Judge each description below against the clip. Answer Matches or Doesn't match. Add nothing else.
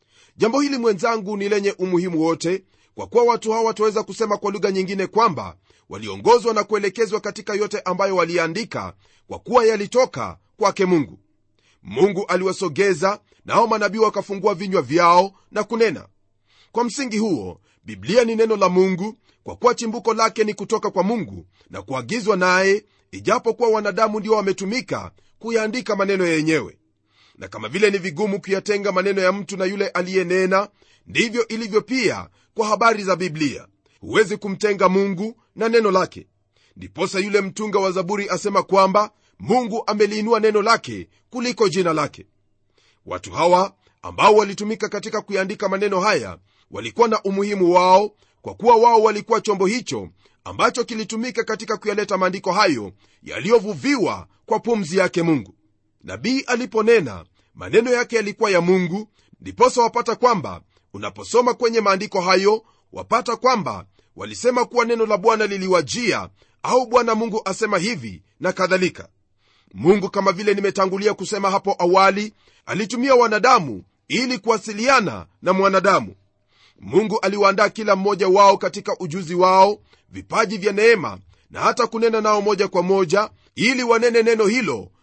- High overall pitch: Matches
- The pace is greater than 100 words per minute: Matches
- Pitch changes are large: Doesn't match